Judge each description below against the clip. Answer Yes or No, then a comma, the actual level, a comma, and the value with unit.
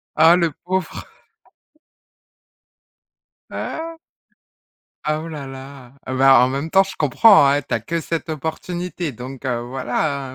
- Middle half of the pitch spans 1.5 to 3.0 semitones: No, average, 4.1 semitones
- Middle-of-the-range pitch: Yes, medium, 145 Hz